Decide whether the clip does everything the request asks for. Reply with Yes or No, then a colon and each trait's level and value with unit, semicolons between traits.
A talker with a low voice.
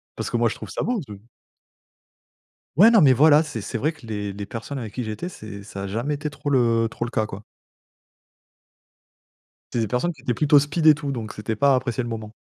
Yes: low, 120 Hz